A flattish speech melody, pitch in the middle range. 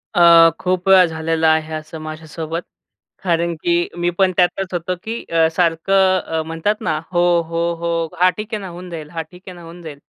Yes: narrow, 2.1 semitones; medium, 170 Hz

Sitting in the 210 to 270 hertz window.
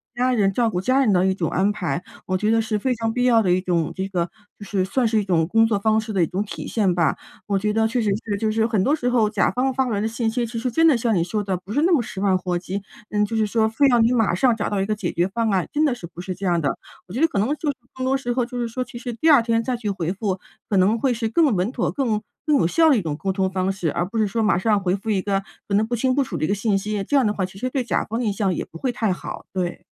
Yes: high, 215 Hz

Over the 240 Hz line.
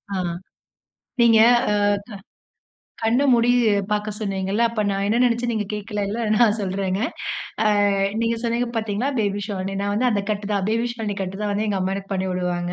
No: high, 210 Hz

